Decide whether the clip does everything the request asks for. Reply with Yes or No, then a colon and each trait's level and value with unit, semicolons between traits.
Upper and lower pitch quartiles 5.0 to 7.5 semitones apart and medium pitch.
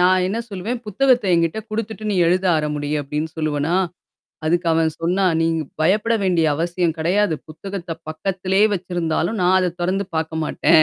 No: average, 3.4 semitones; medium, 175 Hz